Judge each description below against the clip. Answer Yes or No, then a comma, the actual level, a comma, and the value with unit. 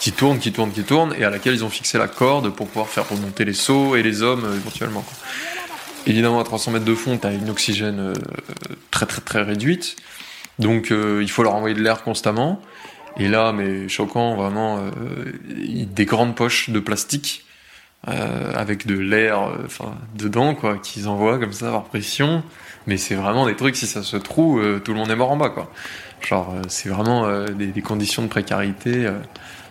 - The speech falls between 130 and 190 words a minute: No, average, 210 wpm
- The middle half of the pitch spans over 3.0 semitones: No, narrow, 2.4 semitones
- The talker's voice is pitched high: No, low, 110 Hz